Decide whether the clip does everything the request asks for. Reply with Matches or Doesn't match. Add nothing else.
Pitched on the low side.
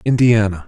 Matches